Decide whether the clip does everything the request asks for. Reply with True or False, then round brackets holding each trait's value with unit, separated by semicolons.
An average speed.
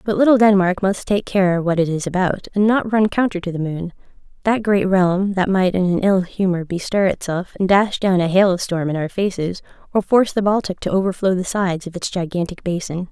False (225 wpm)